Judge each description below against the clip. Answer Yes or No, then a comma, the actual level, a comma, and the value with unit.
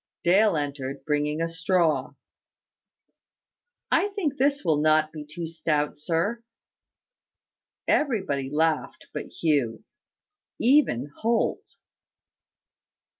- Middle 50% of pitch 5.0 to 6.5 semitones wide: Yes, wide, 5.6 semitones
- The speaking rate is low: Yes, slow, 90 wpm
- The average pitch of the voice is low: No, medium, 160 Hz